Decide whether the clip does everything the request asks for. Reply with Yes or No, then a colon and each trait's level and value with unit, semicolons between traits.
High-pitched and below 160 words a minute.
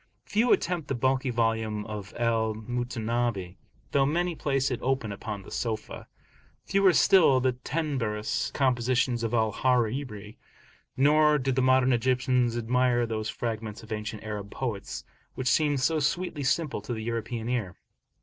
No: low, 120 Hz; average, 150 wpm